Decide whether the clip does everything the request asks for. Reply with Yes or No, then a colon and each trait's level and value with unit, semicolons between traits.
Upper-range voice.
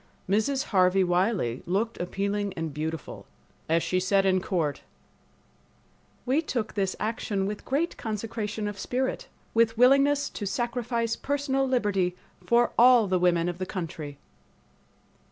Yes: high, 205 Hz